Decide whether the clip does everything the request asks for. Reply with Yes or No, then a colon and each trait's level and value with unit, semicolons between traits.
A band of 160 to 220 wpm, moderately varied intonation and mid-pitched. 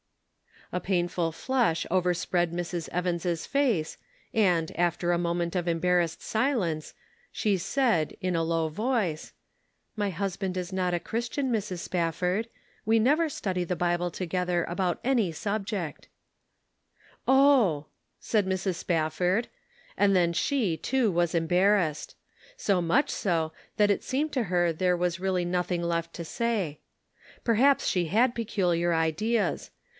No: average, 140 wpm; average, 3.9 semitones; medium, 180 Hz